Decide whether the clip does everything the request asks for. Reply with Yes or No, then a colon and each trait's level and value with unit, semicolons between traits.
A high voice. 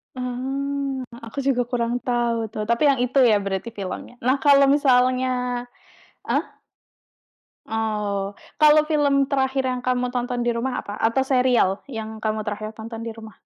Yes: high, 245 Hz